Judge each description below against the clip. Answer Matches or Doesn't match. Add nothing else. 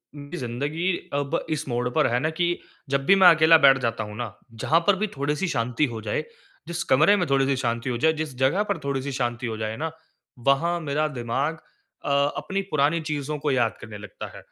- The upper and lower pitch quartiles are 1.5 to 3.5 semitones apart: Doesn't match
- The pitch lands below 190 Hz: Matches